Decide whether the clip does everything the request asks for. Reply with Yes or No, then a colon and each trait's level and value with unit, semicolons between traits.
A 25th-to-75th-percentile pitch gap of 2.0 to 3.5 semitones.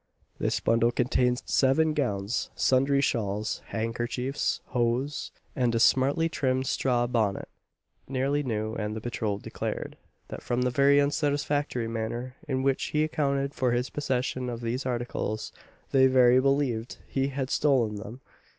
Yes: average, 2.9 semitones